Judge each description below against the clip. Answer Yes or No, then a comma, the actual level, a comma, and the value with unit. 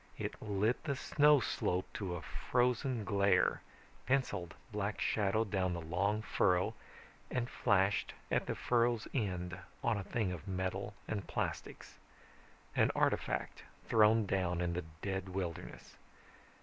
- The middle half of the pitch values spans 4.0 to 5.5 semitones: No, average, 3.5 semitones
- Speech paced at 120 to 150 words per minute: Yes, slow, 135 wpm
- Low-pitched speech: Yes, low, 100 Hz